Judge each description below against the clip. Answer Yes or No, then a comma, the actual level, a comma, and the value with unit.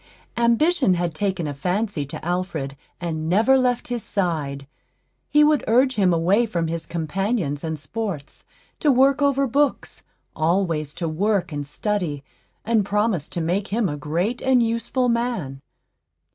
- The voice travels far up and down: Yes, wide, 6.7 semitones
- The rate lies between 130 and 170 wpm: Yes, average, 150 wpm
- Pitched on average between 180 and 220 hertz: Yes, high, 190 Hz